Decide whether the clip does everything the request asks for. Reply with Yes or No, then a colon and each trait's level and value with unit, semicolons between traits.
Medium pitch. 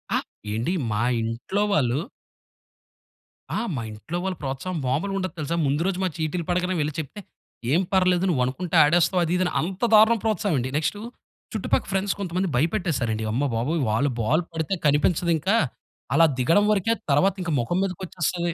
Yes: medium, 170 Hz